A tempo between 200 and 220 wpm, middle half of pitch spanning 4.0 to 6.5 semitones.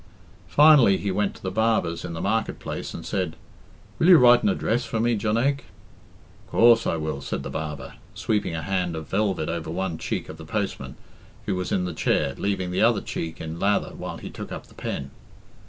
Yes: fast, 205 wpm; average, 5.3 semitones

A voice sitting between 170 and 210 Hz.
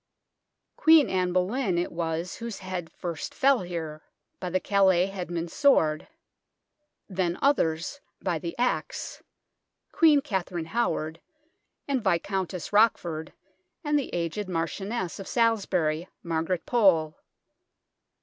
Yes: medium, 185 Hz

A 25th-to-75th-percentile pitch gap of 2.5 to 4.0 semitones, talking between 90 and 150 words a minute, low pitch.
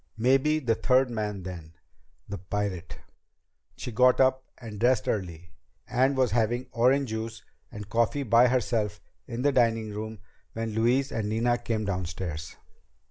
Yes: average, 3.4 semitones; average, 145 wpm; low, 115 Hz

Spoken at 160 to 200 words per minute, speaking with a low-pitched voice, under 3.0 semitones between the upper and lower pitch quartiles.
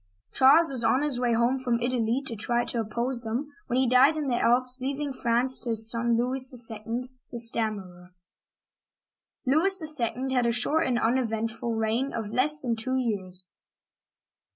No: average, 170 wpm; high, 240 Hz; narrow, 2.5 semitones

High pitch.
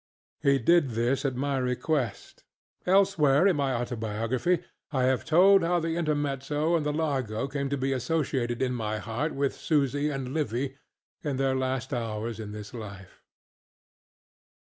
No: low, 135 Hz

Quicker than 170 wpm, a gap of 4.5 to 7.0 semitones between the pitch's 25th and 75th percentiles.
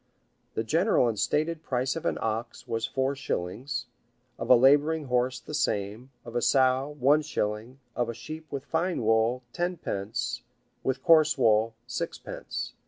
No: average, 155 wpm; average, 4.8 semitones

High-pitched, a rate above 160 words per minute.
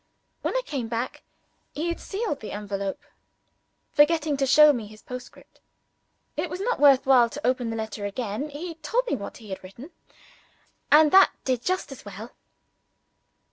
Yes: very high, 260 Hz; average, 170 wpm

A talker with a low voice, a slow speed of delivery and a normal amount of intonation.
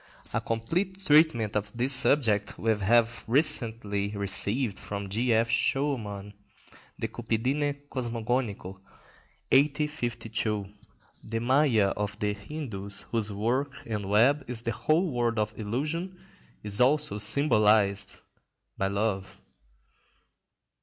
Yes: low, 115 Hz; slow, 110 wpm; average, 4.8 semitones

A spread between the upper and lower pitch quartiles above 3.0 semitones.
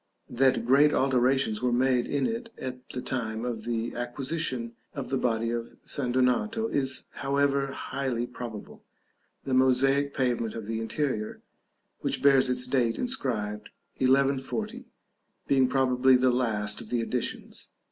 No: narrow, 2.4 semitones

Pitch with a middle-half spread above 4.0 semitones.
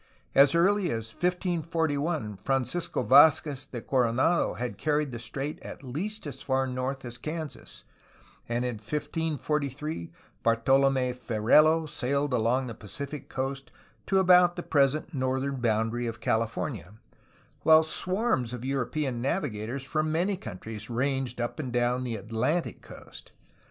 Yes: average, 4.4 semitones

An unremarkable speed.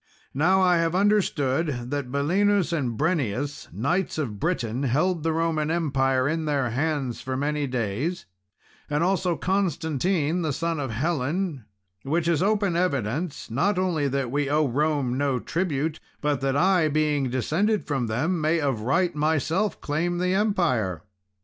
Yes: average, 150 wpm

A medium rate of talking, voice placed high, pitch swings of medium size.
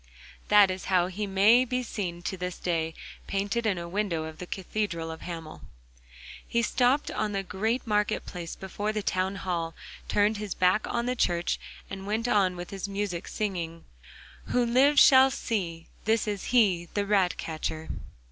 Yes: average, 170 wpm; high, 195 Hz; average, 3.5 semitones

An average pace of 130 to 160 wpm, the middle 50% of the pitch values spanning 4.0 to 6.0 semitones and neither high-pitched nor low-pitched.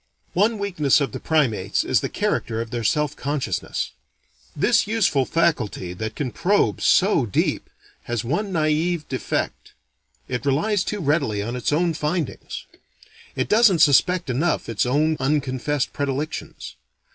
Yes: average, 140 wpm; wide, 5.5 semitones; medium, 150 Hz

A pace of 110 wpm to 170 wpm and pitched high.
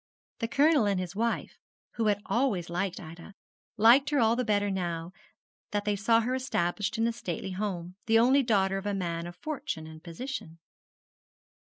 No: average, 180 wpm; high, 205 Hz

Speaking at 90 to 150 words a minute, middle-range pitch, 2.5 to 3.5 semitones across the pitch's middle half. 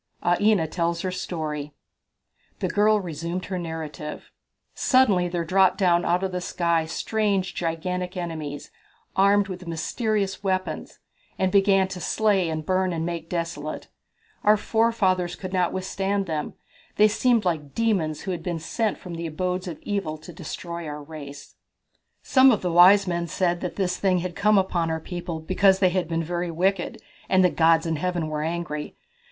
No: average, 170 wpm; medium, 180 Hz; average, 2.8 semitones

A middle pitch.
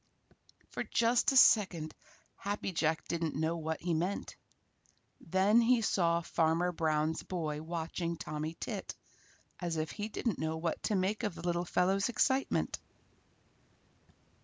Yes: medium, 170 Hz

